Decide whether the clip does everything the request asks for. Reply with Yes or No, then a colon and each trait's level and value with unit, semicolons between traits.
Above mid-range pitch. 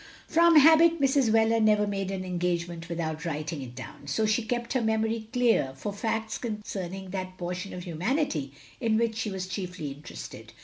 Yes: high, 200 Hz